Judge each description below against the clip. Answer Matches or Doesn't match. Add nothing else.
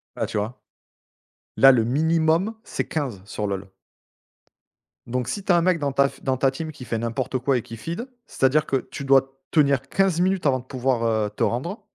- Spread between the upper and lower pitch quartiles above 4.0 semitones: Matches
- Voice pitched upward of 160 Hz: Doesn't match